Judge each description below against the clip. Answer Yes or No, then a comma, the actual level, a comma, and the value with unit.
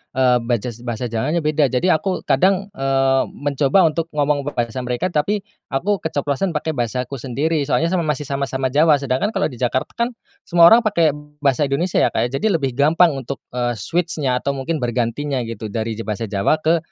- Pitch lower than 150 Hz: Yes, medium, 140 Hz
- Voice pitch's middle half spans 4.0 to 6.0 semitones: Yes, average, 4.6 semitones